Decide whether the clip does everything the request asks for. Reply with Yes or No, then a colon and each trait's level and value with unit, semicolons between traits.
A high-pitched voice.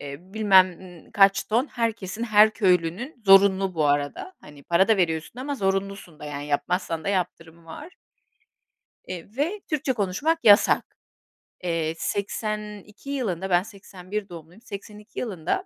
Yes: high, 195 Hz